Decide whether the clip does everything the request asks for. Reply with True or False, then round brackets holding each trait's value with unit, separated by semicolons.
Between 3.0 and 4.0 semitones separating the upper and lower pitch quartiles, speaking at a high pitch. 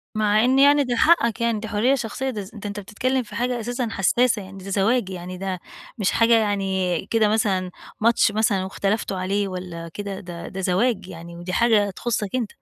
True (3.6 semitones; 205 Hz)